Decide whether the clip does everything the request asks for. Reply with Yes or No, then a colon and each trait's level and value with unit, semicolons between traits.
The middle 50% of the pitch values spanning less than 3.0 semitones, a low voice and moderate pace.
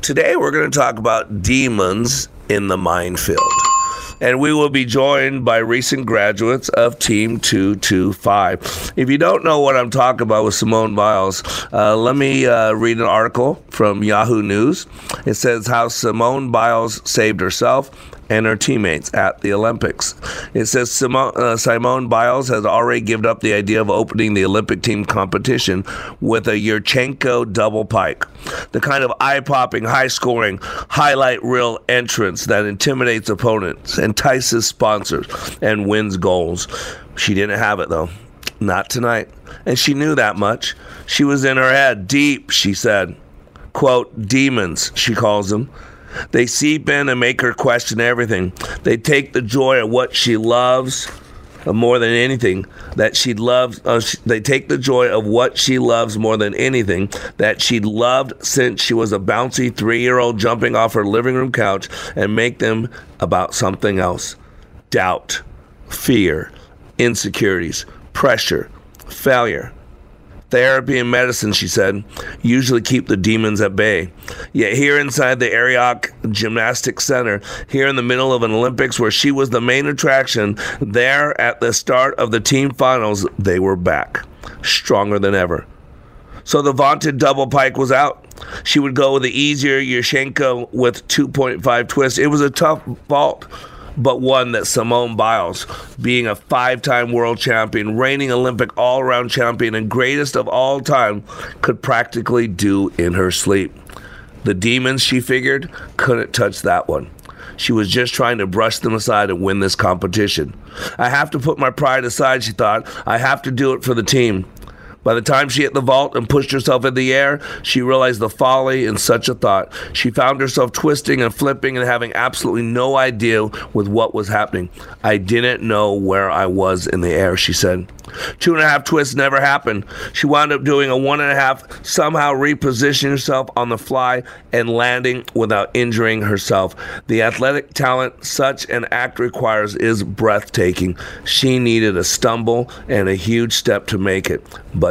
No: average, 3.6 semitones; low, 120 Hz; average, 170 wpm